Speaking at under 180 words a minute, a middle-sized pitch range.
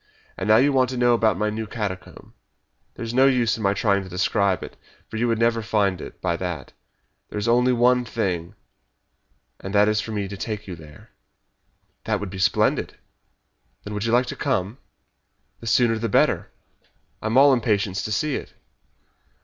No: average, 190 wpm; average, 3.3 semitones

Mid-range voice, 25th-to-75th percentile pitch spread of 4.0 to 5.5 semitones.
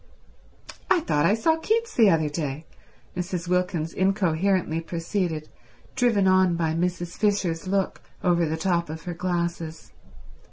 No: medium, 175 Hz; average, 2.8 semitones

